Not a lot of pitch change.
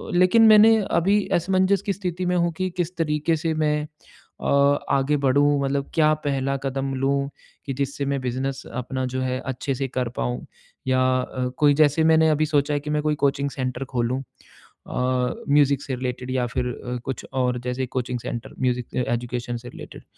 No: average, 3.2 semitones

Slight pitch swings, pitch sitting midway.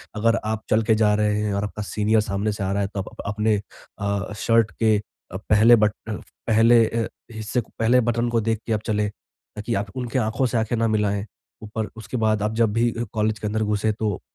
No: narrow, 1.4 semitones; low, 110 Hz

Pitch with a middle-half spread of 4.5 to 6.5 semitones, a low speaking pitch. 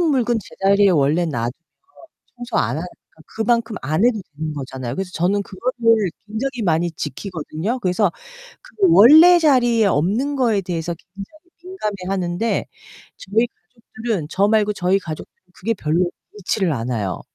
No: wide, 5.5 semitones; high, 200 Hz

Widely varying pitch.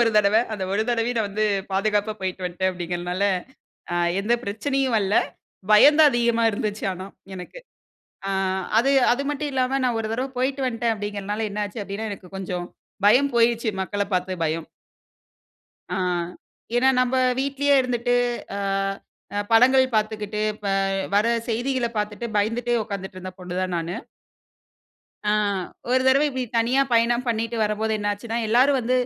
No: average, 3.6 semitones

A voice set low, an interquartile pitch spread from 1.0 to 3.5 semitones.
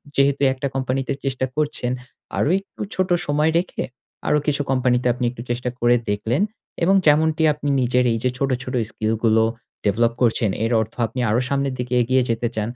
Yes: low, 125 Hz; average, 3.2 semitones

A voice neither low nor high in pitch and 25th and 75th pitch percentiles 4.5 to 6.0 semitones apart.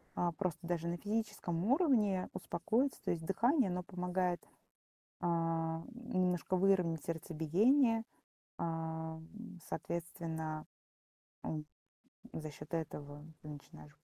No: medium, 175 Hz; average, 3.3 semitones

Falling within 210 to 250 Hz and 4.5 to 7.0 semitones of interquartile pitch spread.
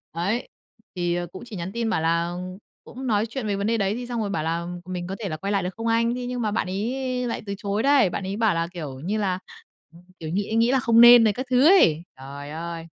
No: high, 200 Hz; average, 5.1 semitones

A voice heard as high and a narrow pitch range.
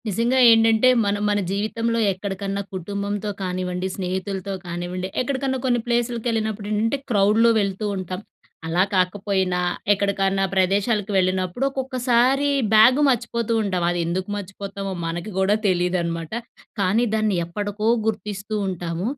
No: high, 200 Hz; average, 3.3 semitones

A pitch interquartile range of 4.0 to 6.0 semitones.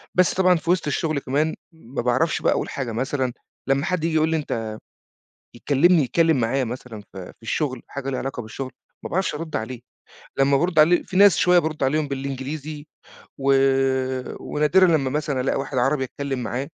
No: average, 3.5 semitones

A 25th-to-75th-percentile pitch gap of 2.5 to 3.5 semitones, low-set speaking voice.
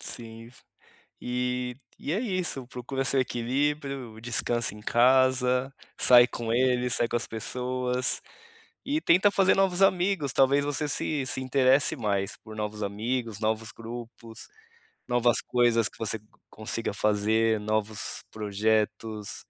Yes: average, 3.2 semitones; low, 120 Hz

